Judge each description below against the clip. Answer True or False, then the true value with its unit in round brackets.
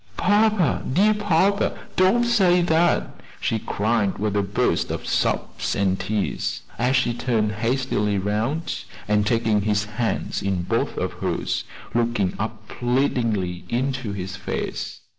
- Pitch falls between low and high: False (115 Hz)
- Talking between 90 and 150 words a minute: True (135 wpm)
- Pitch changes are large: True (7.0 semitones)